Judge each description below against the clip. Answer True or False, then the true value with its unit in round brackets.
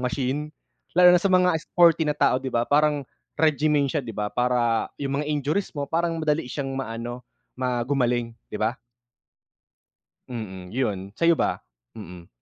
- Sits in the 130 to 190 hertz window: True (135 Hz)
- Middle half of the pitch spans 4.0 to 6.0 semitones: True (4.3 semitones)